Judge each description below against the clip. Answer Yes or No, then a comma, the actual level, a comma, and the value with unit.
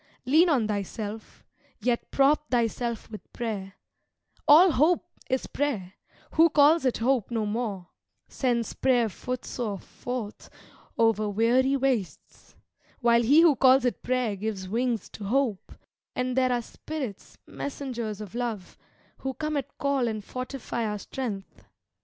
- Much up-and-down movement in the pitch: No, average, 3.8 semitones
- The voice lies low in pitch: No, high, 240 Hz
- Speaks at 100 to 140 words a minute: Yes, slow, 135 wpm